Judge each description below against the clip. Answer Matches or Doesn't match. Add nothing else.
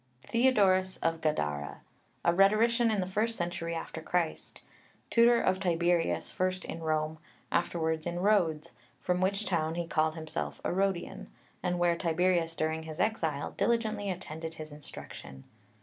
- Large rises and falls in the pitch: Doesn't match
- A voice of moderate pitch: Matches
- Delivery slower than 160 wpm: Matches